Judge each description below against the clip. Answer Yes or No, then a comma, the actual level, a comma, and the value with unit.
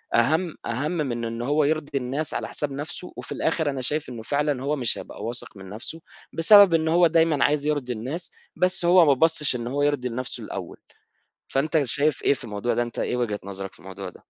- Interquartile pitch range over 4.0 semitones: Yes, average, 4.7 semitones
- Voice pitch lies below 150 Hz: Yes, medium, 140 Hz